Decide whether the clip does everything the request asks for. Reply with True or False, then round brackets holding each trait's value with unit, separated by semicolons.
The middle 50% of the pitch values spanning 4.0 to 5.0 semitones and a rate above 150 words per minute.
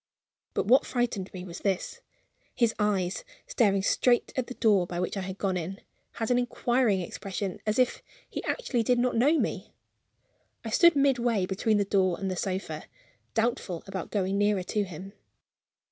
True (4.3 semitones; 175 wpm)